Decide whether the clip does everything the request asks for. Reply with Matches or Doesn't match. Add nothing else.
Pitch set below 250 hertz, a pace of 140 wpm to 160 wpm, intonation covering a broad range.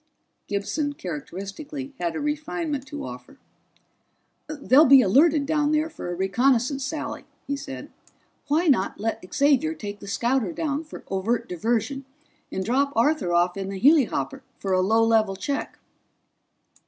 Doesn't match